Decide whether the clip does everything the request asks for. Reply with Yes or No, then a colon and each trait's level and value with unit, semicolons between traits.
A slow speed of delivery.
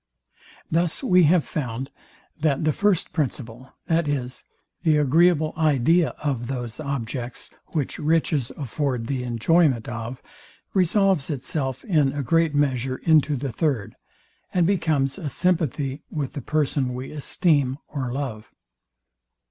Yes: slow, 125 wpm